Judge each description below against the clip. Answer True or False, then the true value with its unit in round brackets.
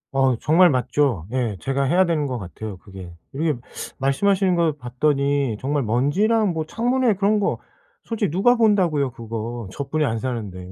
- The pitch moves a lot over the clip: True (7.1 semitones)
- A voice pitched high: False (140 Hz)